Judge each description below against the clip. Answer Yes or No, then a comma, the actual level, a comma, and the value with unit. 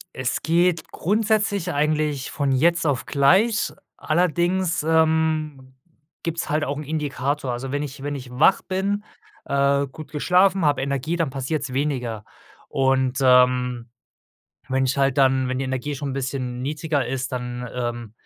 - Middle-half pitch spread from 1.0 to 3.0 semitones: No, average, 3.6 semitones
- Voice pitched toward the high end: No, medium, 140 Hz